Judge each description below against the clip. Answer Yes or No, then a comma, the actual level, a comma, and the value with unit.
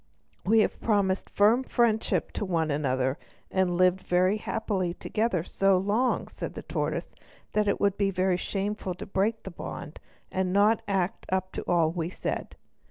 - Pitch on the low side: No, high, 190 Hz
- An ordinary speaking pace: Yes, average, 165 wpm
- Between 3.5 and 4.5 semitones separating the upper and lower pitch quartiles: No, average, 2.9 semitones